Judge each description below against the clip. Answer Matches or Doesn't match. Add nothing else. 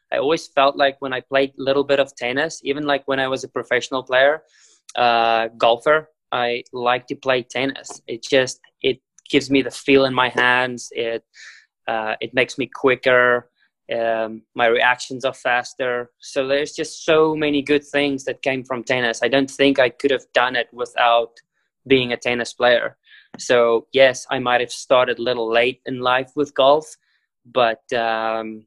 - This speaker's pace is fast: Doesn't match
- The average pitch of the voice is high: Doesn't match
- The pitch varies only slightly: Matches